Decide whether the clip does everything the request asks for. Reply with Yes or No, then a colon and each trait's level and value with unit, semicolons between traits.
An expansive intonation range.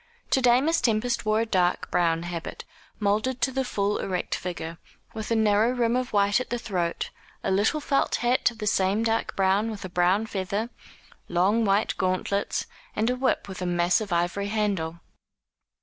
No: average, 3.8 semitones